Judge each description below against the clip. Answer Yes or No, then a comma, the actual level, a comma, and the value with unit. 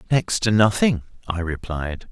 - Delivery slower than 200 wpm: Yes, average, 140 wpm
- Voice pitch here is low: Yes, low, 100 Hz